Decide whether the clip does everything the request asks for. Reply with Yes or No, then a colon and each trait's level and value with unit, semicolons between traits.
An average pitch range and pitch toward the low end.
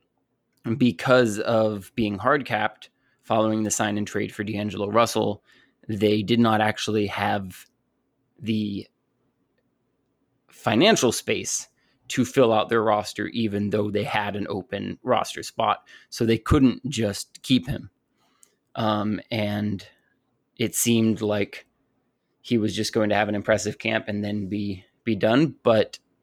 No: narrow, 1.5 semitones; low, 105 Hz